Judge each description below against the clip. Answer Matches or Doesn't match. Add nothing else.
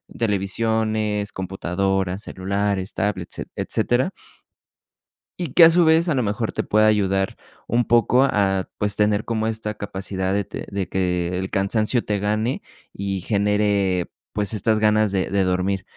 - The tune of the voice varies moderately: Doesn't match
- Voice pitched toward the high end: Doesn't match